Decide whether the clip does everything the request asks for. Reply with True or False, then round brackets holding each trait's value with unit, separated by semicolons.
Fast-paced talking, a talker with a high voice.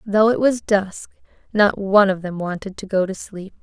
True (215 wpm; 200 Hz)